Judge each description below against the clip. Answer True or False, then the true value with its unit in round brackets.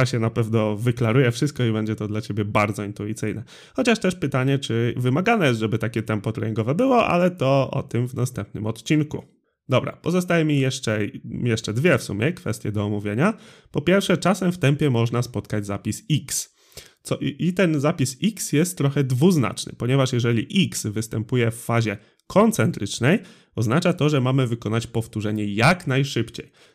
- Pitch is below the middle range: True (125 Hz)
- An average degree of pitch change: False (5.8 semitones)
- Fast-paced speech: True (165 wpm)